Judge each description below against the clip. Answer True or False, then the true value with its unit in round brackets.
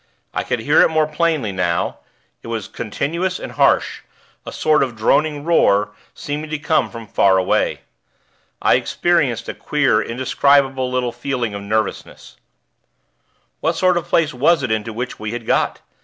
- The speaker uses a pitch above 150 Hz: False (130 Hz)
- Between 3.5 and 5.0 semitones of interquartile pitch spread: False (5.6 semitones)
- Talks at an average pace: True (160 wpm)